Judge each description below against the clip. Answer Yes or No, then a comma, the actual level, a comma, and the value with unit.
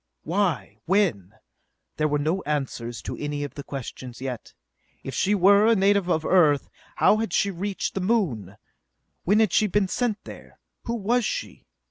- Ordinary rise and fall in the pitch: No, wide, 6.2 semitones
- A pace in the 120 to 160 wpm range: No, average, 170 wpm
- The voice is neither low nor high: Yes, medium, 180 Hz